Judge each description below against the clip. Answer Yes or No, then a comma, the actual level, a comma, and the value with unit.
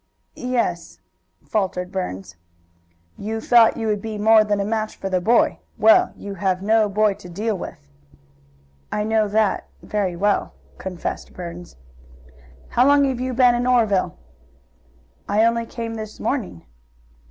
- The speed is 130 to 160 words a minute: Yes, average, 150 wpm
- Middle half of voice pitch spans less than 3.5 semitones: Yes, average, 3.1 semitones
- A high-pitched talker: Yes, high, 215 Hz